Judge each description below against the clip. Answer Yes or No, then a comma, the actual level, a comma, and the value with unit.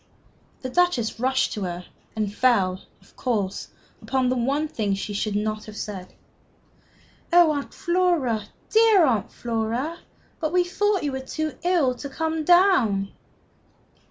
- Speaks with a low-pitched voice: No, very high, 260 Hz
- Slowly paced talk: No, average, 145 wpm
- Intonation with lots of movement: Yes, wide, 7.5 semitones